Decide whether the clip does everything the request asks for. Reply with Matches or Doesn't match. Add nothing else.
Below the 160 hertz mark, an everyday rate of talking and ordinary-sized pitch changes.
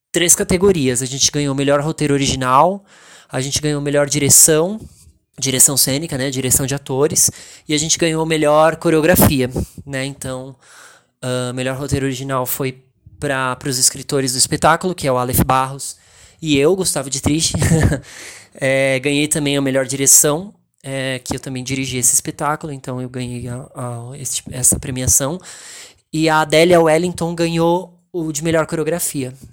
Matches